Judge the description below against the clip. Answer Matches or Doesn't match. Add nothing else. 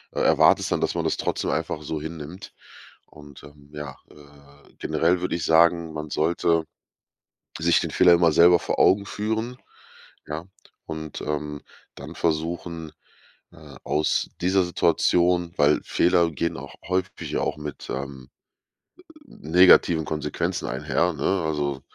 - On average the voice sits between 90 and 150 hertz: Doesn't match